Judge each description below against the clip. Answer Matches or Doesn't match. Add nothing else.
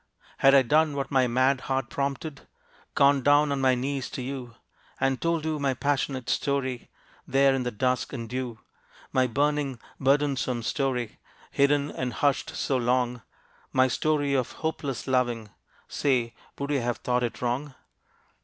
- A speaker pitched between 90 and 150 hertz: Matches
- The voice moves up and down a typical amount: Doesn't match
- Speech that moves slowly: Doesn't match